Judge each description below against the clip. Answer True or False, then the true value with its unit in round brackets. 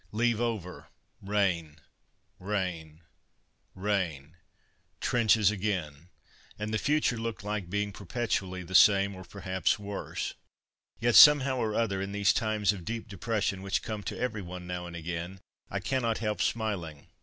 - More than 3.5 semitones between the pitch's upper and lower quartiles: False (3.2 semitones)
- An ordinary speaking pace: True (145 wpm)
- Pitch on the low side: True (100 Hz)